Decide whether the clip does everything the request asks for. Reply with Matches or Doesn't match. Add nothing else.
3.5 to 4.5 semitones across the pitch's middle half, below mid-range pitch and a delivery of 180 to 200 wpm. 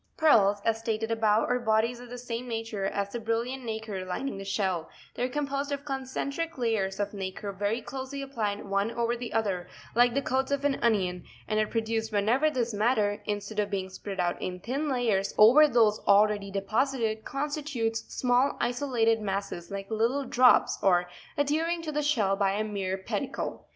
Doesn't match